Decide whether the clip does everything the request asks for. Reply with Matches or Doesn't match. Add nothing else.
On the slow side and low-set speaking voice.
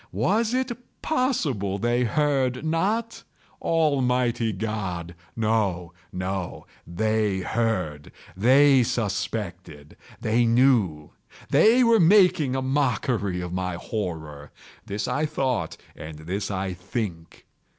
Matches